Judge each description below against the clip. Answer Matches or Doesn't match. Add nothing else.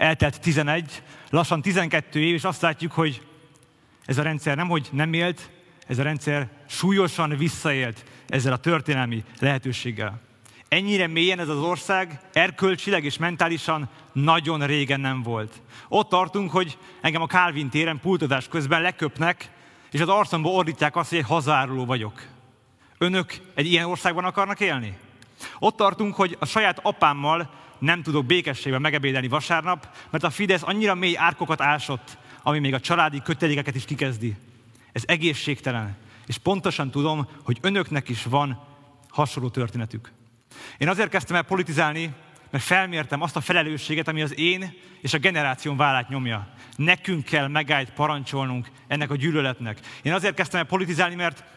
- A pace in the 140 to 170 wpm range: Matches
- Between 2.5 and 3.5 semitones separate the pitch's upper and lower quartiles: Doesn't match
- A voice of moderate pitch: Matches